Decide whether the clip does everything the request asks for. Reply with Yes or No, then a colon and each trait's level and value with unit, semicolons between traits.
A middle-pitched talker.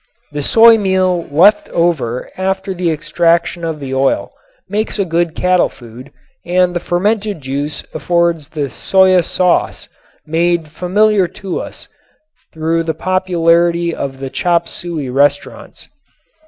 Yes: medium, 170 Hz